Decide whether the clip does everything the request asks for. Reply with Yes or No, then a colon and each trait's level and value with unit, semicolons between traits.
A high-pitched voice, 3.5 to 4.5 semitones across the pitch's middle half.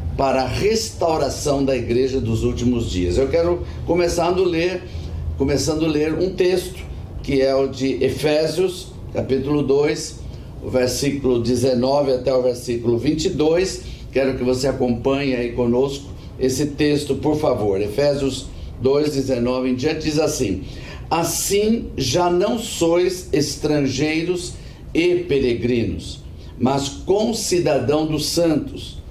No: low, 135 Hz; average, 4.2 semitones